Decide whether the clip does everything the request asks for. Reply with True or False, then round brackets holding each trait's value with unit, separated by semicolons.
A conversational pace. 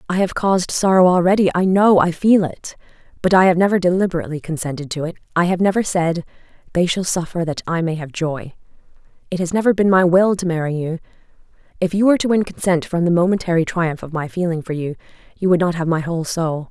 False (210 wpm)